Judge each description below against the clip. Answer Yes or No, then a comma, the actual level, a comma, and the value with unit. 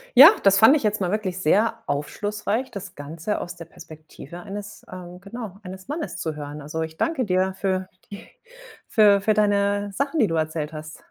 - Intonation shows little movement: No, average, 4.3 semitones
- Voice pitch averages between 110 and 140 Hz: No, high, 190 Hz